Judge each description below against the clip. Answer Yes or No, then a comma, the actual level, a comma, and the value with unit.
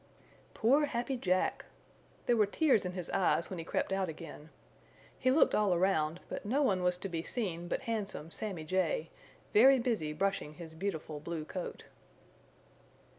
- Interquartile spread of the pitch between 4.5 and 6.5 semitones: Yes, average, 5.1 semitones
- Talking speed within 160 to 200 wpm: Yes, average, 165 wpm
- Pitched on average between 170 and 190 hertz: Yes, medium, 185 Hz